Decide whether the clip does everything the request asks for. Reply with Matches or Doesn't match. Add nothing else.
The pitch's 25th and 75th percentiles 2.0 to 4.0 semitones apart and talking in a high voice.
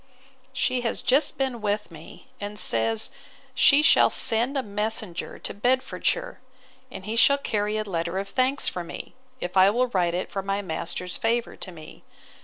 Doesn't match